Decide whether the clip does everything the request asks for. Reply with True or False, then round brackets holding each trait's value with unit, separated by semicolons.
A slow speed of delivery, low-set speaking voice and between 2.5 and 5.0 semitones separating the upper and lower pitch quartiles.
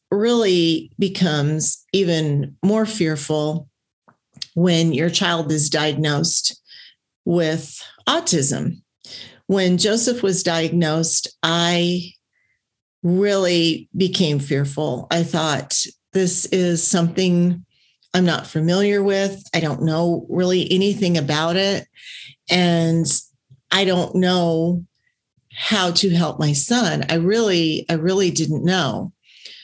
False (105 wpm; 170 Hz; 2.9 semitones)